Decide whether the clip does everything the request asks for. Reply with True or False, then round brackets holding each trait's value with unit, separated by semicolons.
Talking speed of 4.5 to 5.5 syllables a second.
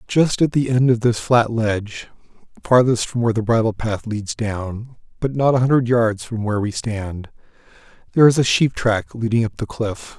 True (5.0 syllables/s)